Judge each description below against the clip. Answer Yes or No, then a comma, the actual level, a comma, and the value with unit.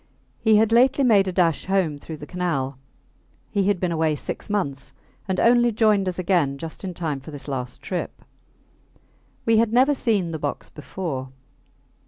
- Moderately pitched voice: Yes, medium, 180 Hz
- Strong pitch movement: Yes, wide, 6.1 semitones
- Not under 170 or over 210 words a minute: Yes, average, 175 wpm